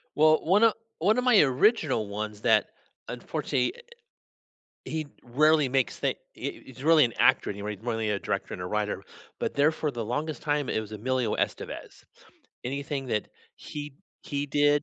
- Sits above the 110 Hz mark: Yes, low, 135 Hz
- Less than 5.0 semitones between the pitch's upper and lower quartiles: No, wide, 5.6 semitones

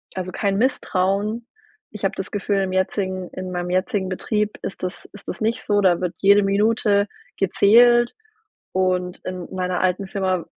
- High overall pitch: Yes, high, 195 Hz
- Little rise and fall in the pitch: Yes, narrow, 2.1 semitones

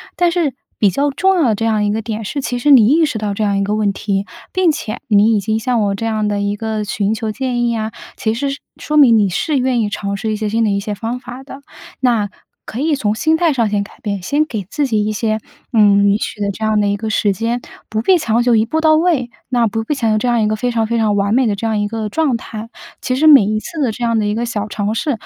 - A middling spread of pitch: Yes, average, 3.4 semitones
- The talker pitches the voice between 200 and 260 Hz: Yes, high, 225 Hz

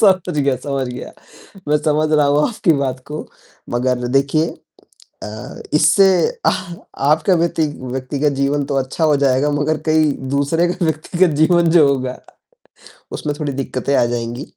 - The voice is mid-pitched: Yes, medium, 145 Hz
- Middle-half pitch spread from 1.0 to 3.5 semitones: Yes, average, 2.9 semitones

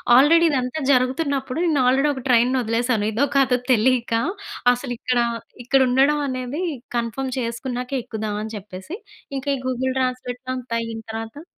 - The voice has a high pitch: Yes, very high, 255 Hz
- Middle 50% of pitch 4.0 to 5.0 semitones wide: No, narrow, 2.4 semitones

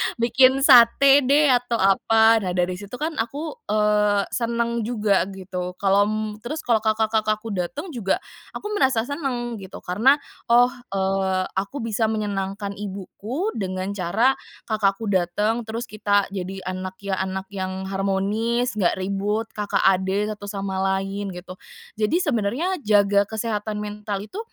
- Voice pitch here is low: No, high, 210 Hz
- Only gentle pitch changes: No, average, 3.3 semitones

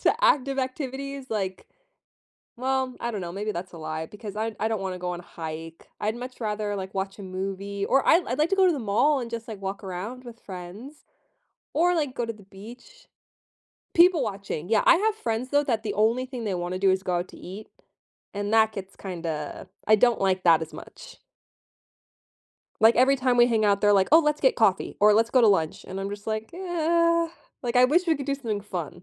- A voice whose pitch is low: No, high, 220 Hz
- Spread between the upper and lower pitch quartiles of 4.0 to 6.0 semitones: Yes, average, 5.3 semitones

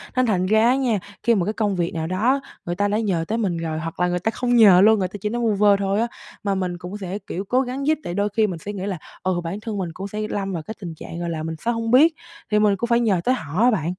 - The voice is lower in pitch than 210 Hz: Yes, high, 200 Hz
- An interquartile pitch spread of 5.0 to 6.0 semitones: No, average, 4.1 semitones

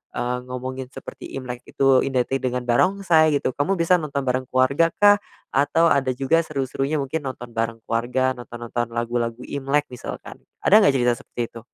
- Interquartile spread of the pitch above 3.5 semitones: No, average, 3.1 semitones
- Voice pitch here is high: No, low, 130 Hz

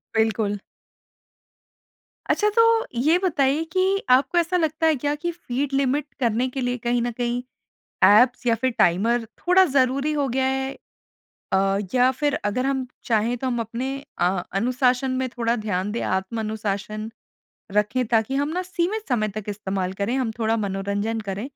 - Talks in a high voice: Yes, high, 245 Hz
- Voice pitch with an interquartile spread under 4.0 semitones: No, average, 4.7 semitones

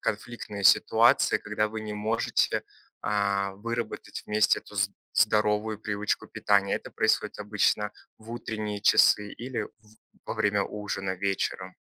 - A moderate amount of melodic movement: No, narrow, 1.1 semitones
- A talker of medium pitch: No, low, 105 Hz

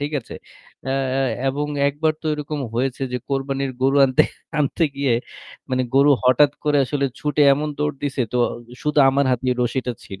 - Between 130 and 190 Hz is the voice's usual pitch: Yes, low, 135 Hz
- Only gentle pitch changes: Yes, narrow, 2.1 semitones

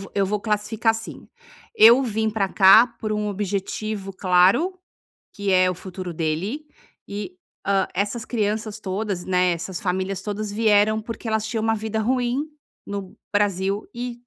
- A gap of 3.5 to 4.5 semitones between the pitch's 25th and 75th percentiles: No, narrow, 2.5 semitones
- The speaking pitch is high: Yes, high, 210 Hz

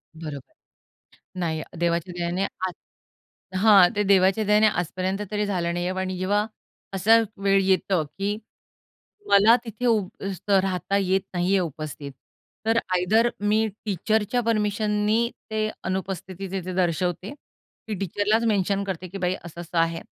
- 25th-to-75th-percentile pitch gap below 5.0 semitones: Yes, average, 2.8 semitones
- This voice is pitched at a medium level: No, high, 195 Hz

